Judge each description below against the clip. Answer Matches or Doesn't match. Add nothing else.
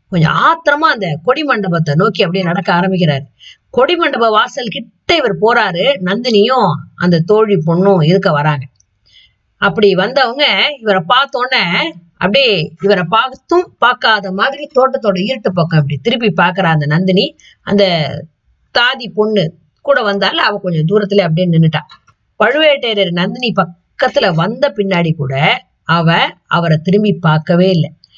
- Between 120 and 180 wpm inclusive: Matches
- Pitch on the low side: Doesn't match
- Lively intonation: Doesn't match